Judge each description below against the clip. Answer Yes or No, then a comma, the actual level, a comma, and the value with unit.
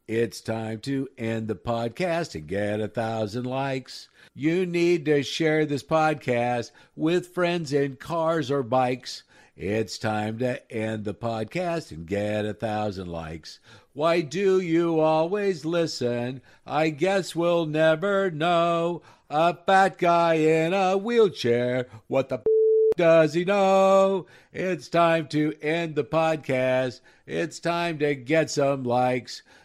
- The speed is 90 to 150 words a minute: Yes, average, 140 wpm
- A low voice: No, medium, 155 Hz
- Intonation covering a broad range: Yes, wide, 5.9 semitones